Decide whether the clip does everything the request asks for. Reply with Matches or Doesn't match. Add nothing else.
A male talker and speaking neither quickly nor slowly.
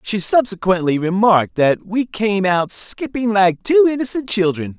Matches